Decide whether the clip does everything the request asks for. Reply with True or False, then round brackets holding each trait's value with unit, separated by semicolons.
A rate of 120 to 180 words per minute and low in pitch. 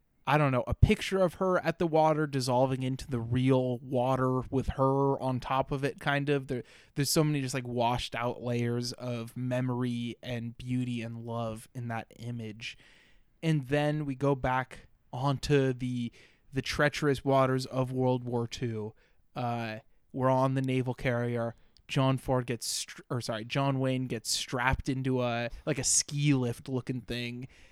True (170 wpm; 130 Hz)